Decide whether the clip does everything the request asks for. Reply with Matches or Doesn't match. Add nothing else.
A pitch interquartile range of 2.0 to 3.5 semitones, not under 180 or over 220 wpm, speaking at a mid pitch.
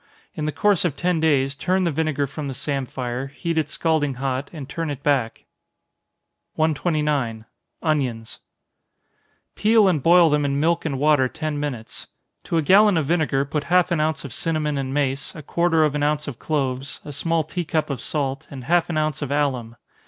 Matches